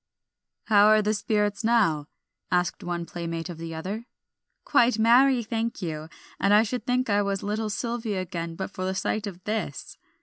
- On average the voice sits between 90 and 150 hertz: No, high, 205 Hz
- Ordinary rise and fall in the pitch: Yes, average, 4.1 semitones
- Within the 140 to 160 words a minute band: No, average, 175 wpm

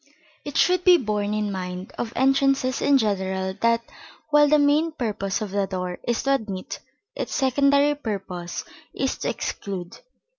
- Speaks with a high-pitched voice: Yes, high, 225 Hz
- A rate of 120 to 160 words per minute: Yes, average, 155 wpm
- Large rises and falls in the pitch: Yes, wide, 6.5 semitones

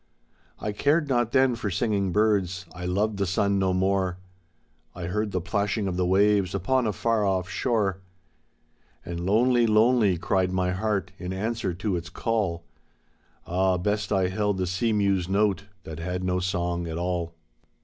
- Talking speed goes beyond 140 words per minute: Yes, average, 170 wpm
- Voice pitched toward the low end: Yes, very low, 95 Hz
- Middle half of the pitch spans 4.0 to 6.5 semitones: No, average, 2.8 semitones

